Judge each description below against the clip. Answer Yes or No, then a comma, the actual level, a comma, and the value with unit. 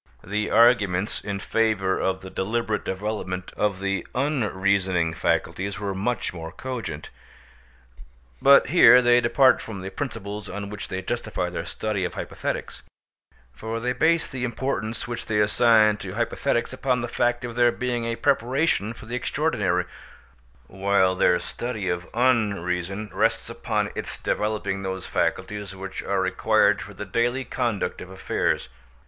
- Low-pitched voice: Yes, low, 105 Hz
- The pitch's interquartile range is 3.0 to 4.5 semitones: Yes, average, 3.9 semitones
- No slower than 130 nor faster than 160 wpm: Yes, average, 150 wpm